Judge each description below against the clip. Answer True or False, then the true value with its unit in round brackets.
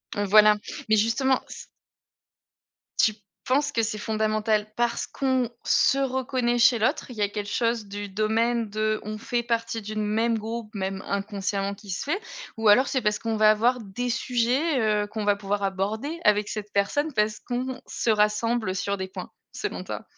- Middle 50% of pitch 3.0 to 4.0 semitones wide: False (2.6 semitones)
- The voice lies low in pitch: False (215 Hz)